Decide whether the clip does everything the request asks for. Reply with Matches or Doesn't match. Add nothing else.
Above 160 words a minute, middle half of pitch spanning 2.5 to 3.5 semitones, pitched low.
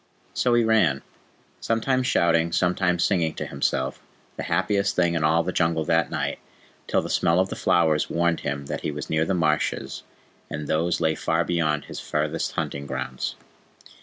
Matches